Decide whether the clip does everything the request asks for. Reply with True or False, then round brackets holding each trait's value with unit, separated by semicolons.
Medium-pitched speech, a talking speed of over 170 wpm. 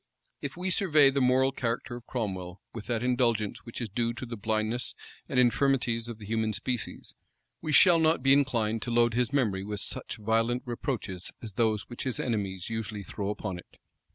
False (115 Hz; 190 wpm)